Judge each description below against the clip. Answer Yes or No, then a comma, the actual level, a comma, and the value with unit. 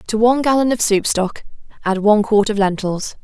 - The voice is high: Yes, high, 215 Hz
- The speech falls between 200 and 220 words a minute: Yes, fast, 205 wpm